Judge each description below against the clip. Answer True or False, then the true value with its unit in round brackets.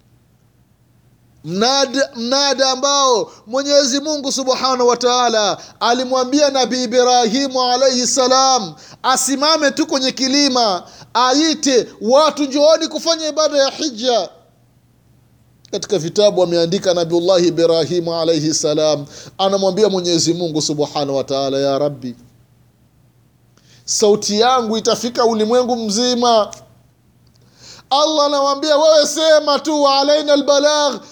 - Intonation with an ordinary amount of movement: False (8.0 semitones)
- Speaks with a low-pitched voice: False (245 Hz)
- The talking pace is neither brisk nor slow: False (95 wpm)